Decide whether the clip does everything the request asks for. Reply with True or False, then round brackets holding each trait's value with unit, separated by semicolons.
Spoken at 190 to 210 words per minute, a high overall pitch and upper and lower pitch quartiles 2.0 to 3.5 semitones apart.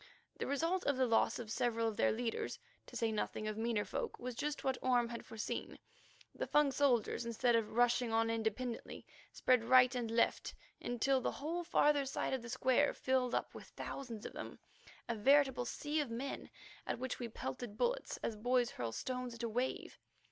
True (195 wpm; 245 Hz; 2.6 semitones)